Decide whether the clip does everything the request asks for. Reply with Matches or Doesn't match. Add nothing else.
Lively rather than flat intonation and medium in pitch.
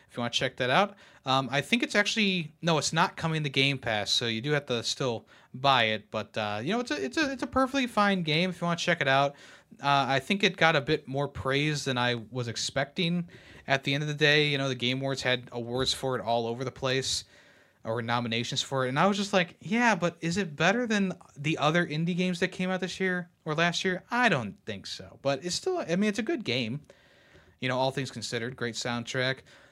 Matches